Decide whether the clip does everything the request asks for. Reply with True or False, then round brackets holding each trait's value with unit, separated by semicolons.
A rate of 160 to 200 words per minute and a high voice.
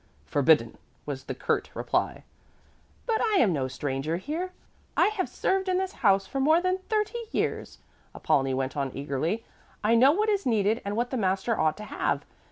True (180 wpm; 220 Hz)